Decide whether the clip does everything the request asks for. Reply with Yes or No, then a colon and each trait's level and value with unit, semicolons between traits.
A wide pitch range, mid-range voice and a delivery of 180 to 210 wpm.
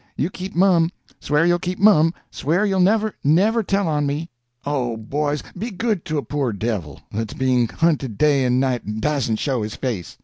Yes: wide, 6.4 semitones; medium, 150 Hz; average, 190 wpm